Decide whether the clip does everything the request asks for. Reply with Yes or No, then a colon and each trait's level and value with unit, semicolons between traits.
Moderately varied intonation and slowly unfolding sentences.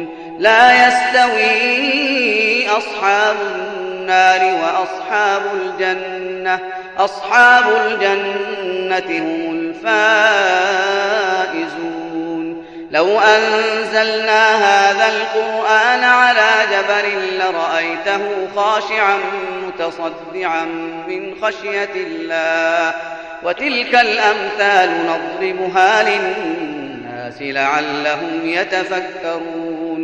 Yes: average, 4.1 semitones; slow, 55 wpm